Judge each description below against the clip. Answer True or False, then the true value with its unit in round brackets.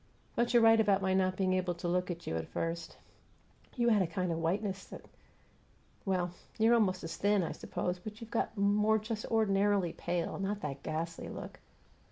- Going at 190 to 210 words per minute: True (195 wpm)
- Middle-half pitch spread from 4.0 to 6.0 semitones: False (3.4 semitones)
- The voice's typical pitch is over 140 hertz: True (190 Hz)